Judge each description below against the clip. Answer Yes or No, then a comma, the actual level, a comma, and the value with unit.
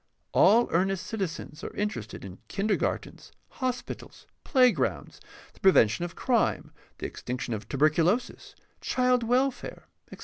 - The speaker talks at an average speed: No, slow, 125 wpm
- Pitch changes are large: Yes, wide, 8.1 semitones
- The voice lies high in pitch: Yes, high, 195 Hz